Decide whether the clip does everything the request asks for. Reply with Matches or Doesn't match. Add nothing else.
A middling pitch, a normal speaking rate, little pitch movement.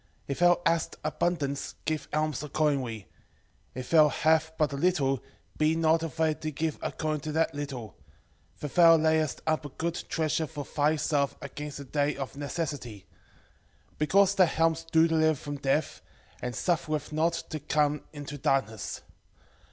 Matches